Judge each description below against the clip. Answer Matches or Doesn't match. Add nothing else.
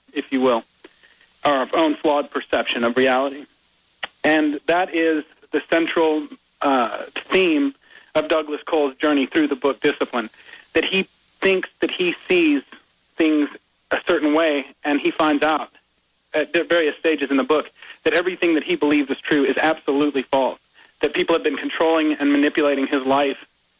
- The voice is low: Doesn't match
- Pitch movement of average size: Matches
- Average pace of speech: Matches